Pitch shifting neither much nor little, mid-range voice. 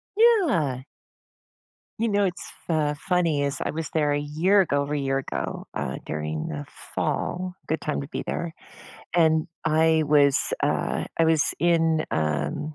Yes: average, 3.2 semitones; medium, 155 Hz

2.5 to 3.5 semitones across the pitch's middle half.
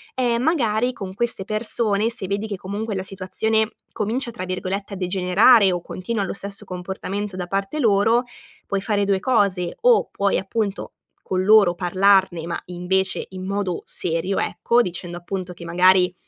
Yes: average, 2.8 semitones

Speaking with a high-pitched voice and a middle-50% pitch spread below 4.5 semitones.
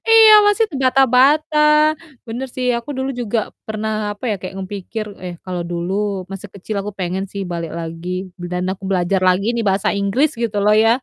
No: high, 205 Hz; wide, 5.5 semitones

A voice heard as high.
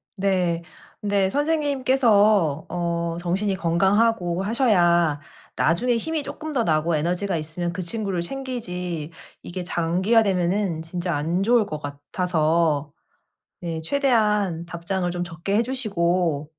No: medium, 180 Hz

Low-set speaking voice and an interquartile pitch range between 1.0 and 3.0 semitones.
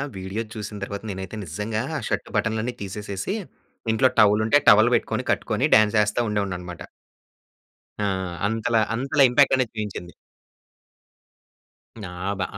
Yes: low, 105 Hz; narrow, 2.5 semitones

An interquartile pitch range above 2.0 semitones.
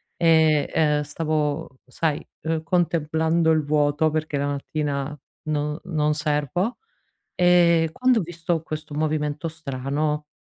No: narrow, 1.7 semitones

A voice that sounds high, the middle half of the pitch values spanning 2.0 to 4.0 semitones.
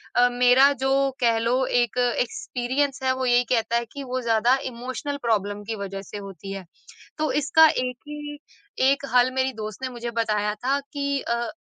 Yes: high, 245 Hz; average, 2.9 semitones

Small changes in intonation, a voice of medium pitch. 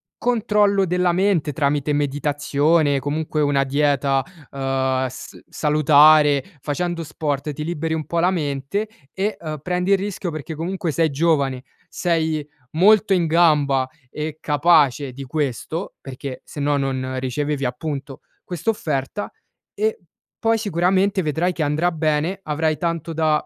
No: average, 3.5 semitones; medium, 155 Hz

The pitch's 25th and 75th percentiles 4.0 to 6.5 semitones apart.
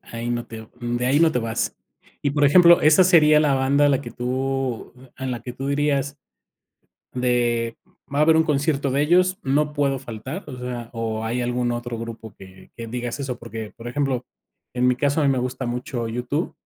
No: average, 3.2 semitones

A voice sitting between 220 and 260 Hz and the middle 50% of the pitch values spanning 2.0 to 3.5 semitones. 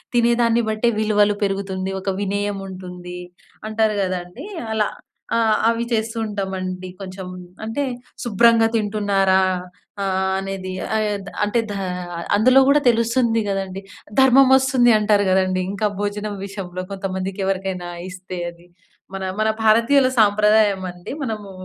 No: high, 205 Hz; average, 2.8 semitones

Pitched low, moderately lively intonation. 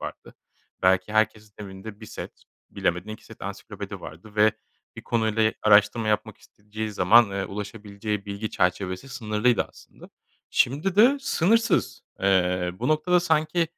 Yes: low, 110 Hz; average, 3.6 semitones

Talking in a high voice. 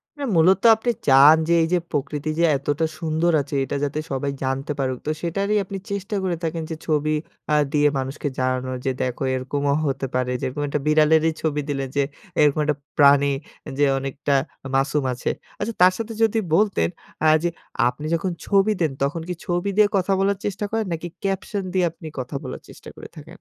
No: medium, 155 Hz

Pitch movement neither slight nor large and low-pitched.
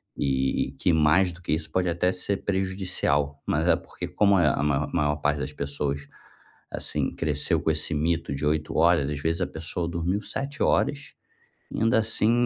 Yes: average, 4.0 semitones; very low, 80 Hz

